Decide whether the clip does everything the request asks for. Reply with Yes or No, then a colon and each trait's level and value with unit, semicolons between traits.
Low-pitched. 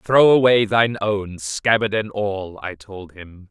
Yes: low, 100 Hz